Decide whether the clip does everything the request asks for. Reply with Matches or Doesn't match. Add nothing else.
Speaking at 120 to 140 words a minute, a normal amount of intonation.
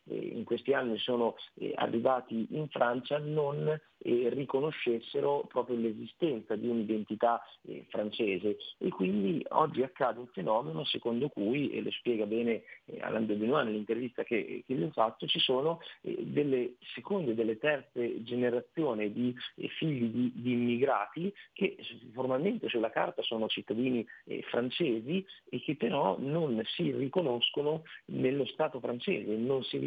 Matches